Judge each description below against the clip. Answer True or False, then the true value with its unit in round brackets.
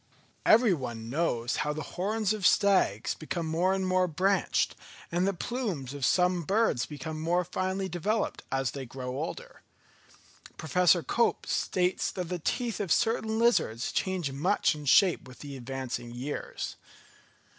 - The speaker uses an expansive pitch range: True (5.7 semitones)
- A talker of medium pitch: True (175 Hz)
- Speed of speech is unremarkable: True (145 wpm)